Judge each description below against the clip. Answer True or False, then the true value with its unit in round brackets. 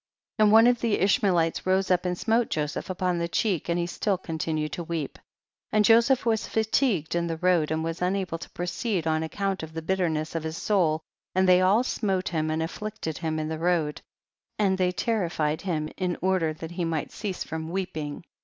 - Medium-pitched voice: True (175 Hz)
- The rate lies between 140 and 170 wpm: False (205 wpm)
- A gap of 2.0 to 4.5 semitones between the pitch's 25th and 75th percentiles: True (3.3 semitones)